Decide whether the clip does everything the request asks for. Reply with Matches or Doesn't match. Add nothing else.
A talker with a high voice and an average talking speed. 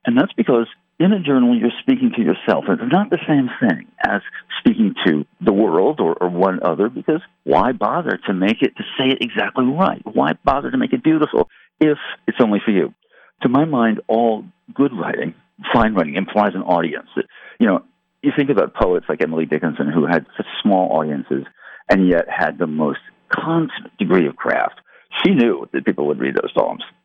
Doesn't match